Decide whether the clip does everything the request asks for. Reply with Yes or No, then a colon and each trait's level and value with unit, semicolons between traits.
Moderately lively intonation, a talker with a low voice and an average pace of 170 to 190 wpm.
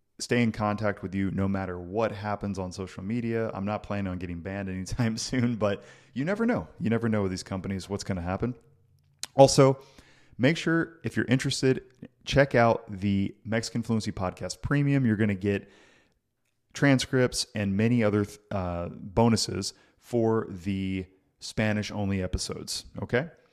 No: average, 3.7 semitones; low, 110 Hz; average, 160 wpm